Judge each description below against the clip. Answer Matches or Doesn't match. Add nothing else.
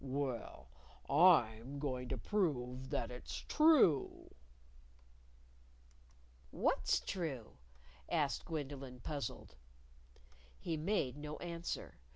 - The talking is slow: Matches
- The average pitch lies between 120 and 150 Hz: Matches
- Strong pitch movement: Doesn't match